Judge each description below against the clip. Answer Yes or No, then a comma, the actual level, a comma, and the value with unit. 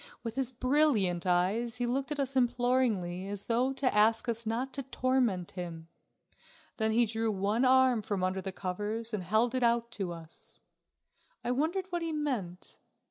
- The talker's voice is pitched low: No, high, 230 Hz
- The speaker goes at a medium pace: Yes, average, 175 wpm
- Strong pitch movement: No, average, 4.8 semitones